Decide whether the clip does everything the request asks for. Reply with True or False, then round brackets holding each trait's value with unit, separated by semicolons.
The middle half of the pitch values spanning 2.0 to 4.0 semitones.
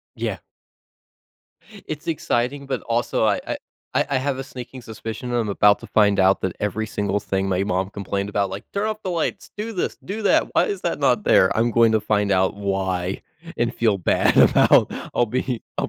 False (4.8 semitones)